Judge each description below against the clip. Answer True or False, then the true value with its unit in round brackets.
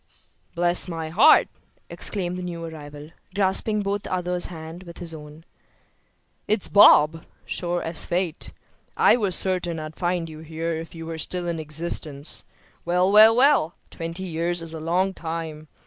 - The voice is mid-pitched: True (170 Hz)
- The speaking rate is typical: True (160 wpm)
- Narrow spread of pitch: True (2.1 semitones)